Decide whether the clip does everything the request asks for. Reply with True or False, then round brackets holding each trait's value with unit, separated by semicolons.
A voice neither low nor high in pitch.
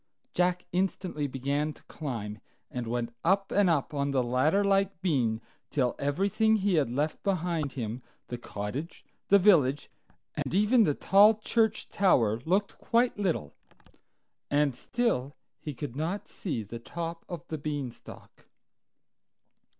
True (155 Hz)